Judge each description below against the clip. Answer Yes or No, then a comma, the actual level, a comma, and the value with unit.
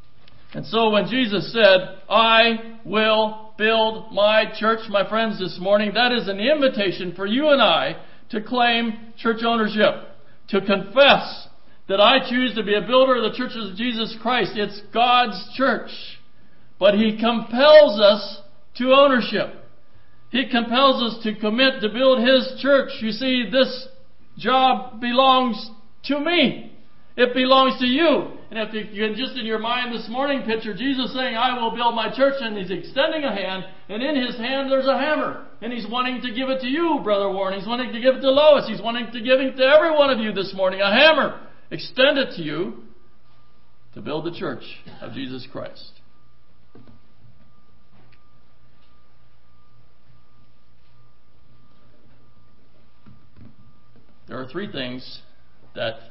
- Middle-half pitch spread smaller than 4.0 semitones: No, average, 4.6 semitones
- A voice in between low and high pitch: No, high, 225 Hz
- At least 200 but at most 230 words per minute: No, average, 155 wpm